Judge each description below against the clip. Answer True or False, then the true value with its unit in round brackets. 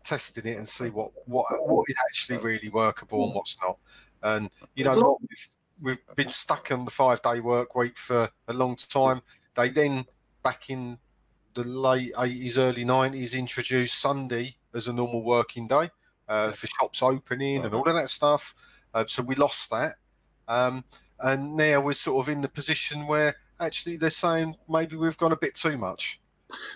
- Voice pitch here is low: True (130 Hz)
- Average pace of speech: True (180 wpm)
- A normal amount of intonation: True (3.0 semitones)